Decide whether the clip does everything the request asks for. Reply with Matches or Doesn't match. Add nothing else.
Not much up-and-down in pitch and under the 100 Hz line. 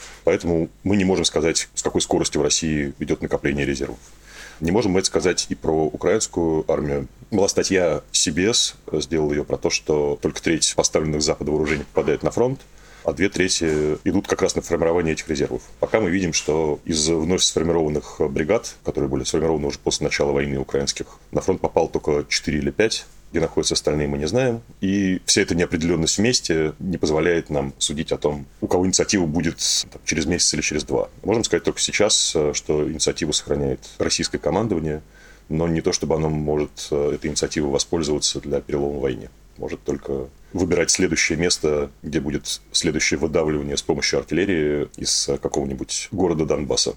Matches